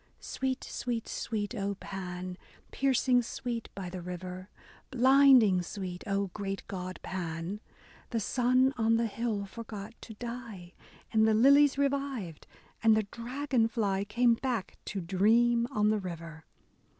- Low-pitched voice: No, high, 215 Hz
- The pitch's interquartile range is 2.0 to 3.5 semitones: No, average, 4.2 semitones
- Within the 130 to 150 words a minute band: Yes, average, 140 wpm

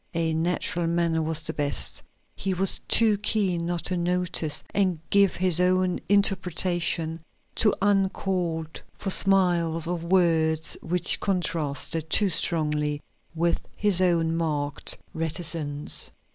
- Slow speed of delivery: Yes, slow, 115 wpm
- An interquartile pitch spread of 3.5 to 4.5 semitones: No, narrow, 2.5 semitones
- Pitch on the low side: No, medium, 170 Hz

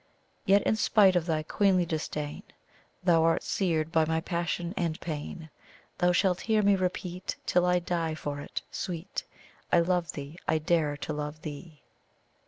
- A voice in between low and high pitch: Yes, medium, 170 Hz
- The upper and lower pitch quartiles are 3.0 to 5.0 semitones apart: No, narrow, 2.4 semitones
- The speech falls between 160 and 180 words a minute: Yes, average, 165 wpm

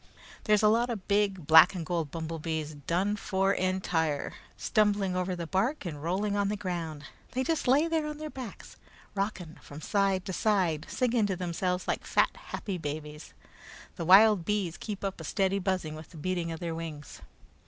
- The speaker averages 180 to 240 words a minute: Yes, average, 185 wpm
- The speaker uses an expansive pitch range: No, average, 3.9 semitones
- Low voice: No, medium, 185 Hz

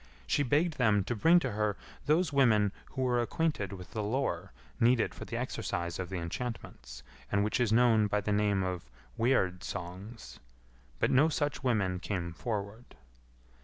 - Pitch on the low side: Yes, low, 110 Hz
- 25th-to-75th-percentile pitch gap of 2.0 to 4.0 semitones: No, average, 4.5 semitones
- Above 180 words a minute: No, average, 165 wpm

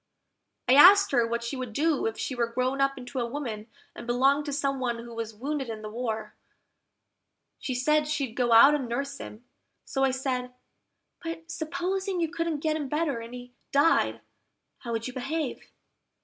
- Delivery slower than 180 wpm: No, average, 190 wpm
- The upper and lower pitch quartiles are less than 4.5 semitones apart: Yes, average, 3.9 semitones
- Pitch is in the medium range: No, very high, 265 Hz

